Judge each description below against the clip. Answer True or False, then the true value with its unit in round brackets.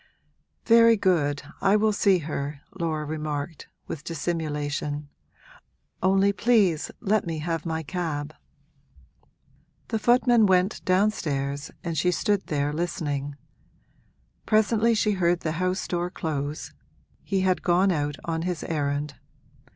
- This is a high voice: False (170 Hz)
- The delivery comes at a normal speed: False (120 wpm)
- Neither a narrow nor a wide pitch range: True (4.6 semitones)